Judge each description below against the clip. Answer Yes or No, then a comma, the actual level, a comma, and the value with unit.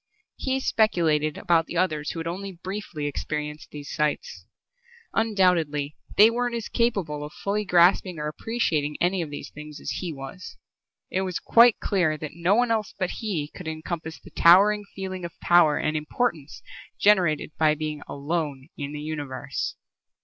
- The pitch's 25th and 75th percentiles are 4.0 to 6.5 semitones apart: Yes, average, 4.4 semitones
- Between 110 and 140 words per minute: No, average, 165 wpm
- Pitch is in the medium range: Yes, medium, 165 Hz